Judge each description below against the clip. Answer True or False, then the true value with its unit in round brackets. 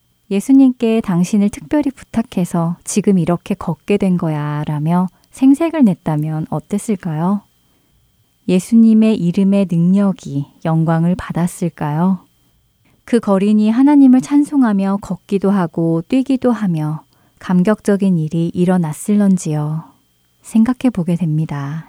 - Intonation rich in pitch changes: False (4.6 semitones)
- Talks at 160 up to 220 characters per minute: False (270 characters per minute)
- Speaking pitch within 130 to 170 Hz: False (185 Hz)